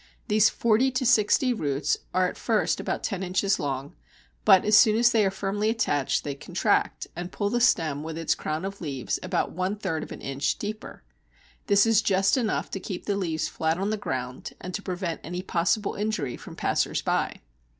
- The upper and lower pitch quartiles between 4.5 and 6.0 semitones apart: Yes, average, 4.9 semitones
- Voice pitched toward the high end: Yes, high, 195 Hz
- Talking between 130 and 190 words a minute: No, average, 200 wpm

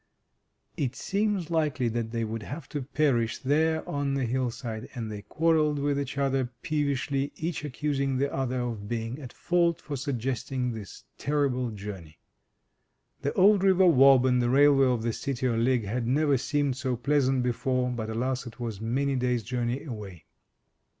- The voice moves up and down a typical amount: Yes, average, 3.4 semitones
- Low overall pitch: Yes, low, 130 Hz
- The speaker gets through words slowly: No, average, 170 wpm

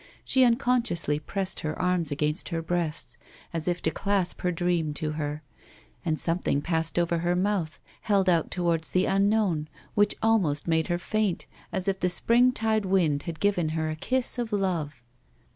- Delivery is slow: No, average, 170 wpm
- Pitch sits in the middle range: Yes, medium, 175 Hz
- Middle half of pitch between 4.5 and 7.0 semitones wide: No, average, 4.0 semitones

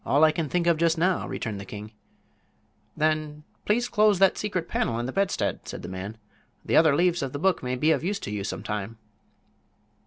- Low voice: No, medium, 155 Hz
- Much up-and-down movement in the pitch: Yes, wide, 7.4 semitones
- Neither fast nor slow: No, fast, 215 wpm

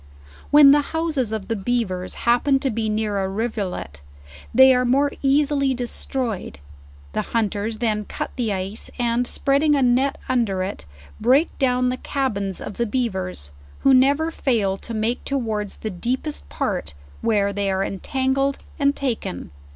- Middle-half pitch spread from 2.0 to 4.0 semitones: No, average, 4.8 semitones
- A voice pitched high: Yes, high, 235 Hz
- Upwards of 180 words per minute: No, average, 160 wpm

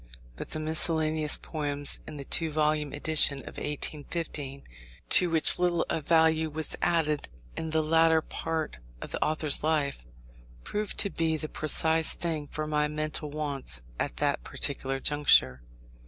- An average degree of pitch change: No, narrow, 1.6 semitones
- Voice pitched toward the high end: No, medium, 155 Hz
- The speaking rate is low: No, average, 150 wpm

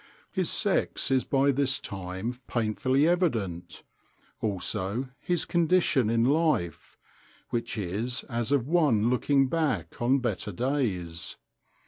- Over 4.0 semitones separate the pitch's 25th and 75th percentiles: Yes, average, 5.1 semitones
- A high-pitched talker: No, low, 125 Hz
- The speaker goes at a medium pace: No, slow, 115 wpm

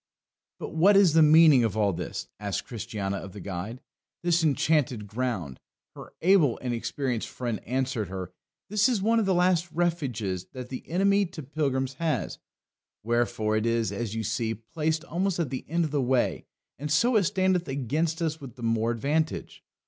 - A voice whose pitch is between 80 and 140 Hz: Yes, low, 135 Hz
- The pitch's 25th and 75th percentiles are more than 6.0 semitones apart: Yes, wide, 6.6 semitones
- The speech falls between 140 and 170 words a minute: No, average, 180 wpm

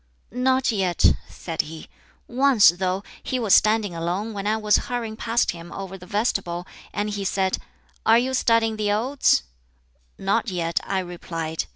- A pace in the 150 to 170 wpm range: Yes, average, 160 wpm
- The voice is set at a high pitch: Yes, high, 205 Hz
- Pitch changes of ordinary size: Yes, average, 4.1 semitones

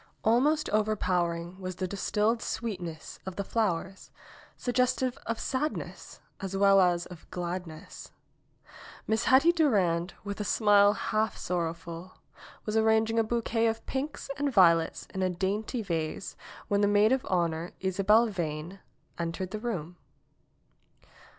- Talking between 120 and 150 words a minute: Yes, slow, 135 wpm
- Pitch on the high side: Yes, high, 200 Hz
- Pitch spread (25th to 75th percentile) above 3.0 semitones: Yes, average, 4.1 semitones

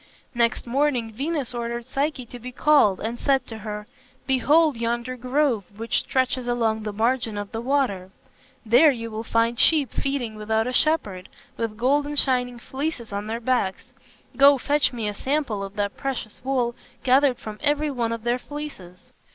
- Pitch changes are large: No, average, 3.7 semitones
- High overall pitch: Yes, high, 240 Hz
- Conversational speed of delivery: Yes, average, 170 wpm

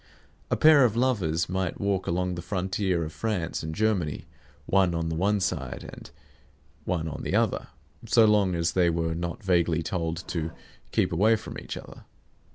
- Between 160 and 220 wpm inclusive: Yes, average, 175 wpm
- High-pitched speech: No, very low, 90 Hz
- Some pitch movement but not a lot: Yes, average, 3.4 semitones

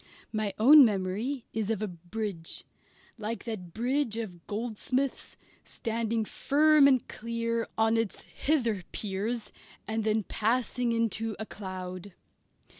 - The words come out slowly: Yes, slow, 120 wpm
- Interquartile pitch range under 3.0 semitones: Yes, narrow, 2.4 semitones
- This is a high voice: Yes, high, 225 Hz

